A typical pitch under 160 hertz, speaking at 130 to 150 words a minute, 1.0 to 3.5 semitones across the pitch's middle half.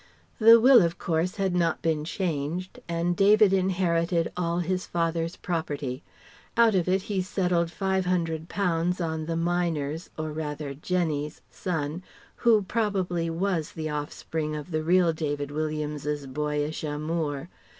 No: medium, 165 Hz; slow, 135 wpm; average, 3.1 semitones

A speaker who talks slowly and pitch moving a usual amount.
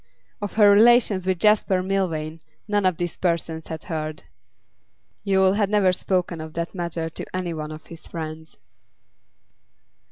No: average, 150 wpm; average, 3.3 semitones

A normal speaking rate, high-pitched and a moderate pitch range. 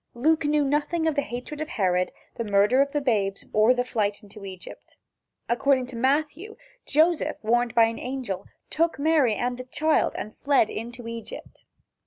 Yes: average, 175 wpm; very high, 250 Hz; average, 4.9 semitones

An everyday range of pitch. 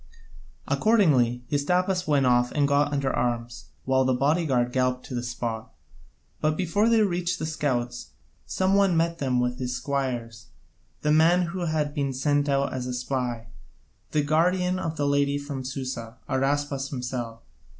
Yes: average, 4.1 semitones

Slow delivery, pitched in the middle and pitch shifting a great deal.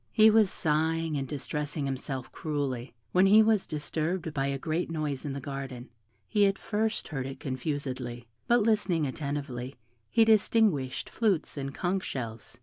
No: average, 155 wpm; medium, 150 Hz; wide, 5.8 semitones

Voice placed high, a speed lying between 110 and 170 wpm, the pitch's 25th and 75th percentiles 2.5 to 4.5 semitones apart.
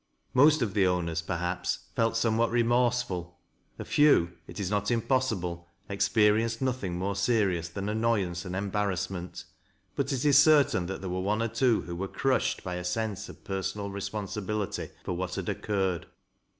No: low, 100 Hz; average, 165 wpm; average, 4.2 semitones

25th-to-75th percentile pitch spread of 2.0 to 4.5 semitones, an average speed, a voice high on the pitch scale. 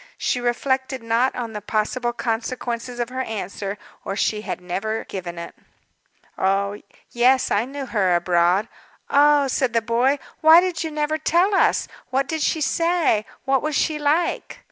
No: average, 5.0 semitones; average, 160 wpm; very high, 250 Hz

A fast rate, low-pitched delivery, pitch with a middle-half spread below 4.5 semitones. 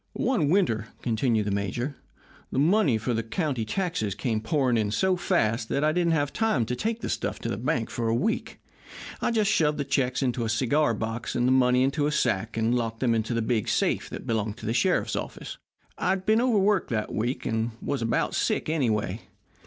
No: fast, 215 wpm; low, 125 Hz; wide, 5.4 semitones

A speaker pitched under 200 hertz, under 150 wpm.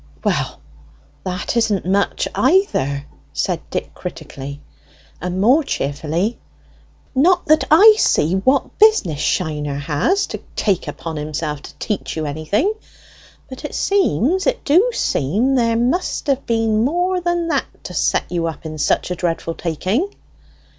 No: high, 205 Hz; average, 140 wpm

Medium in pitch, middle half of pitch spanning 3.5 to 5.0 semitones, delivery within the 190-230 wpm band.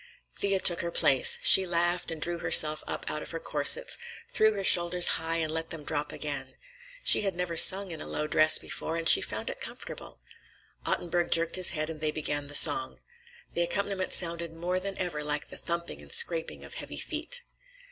No: medium, 170 Hz; average, 2.7 semitones; average, 200 wpm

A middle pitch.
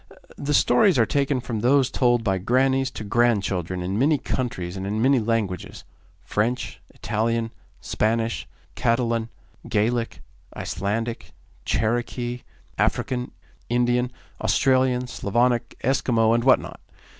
No: low, 120 Hz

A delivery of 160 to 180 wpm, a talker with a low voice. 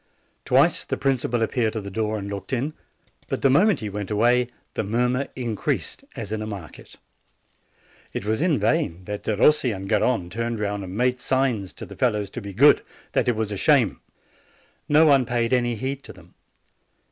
No: average, 195 wpm; low, 115 Hz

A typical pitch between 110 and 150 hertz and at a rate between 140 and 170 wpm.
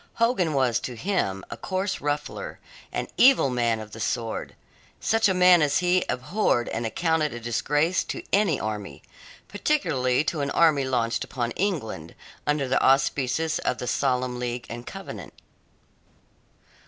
Yes: low, 135 Hz; average, 150 wpm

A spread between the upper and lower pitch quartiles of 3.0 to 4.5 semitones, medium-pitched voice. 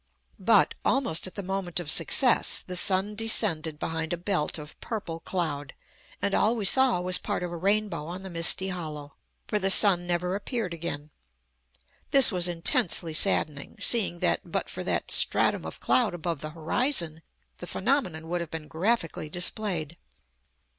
Yes: average, 3.7 semitones; medium, 175 Hz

